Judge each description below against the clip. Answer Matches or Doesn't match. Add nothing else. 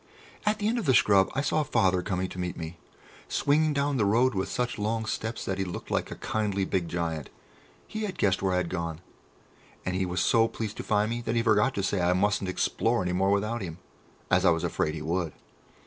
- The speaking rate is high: Matches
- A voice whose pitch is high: Doesn't match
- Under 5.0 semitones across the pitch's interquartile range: Matches